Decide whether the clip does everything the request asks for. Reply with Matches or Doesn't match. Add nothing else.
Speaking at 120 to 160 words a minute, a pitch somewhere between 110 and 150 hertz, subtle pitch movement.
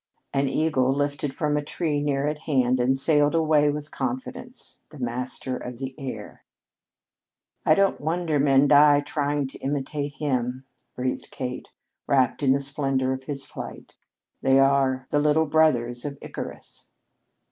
Matches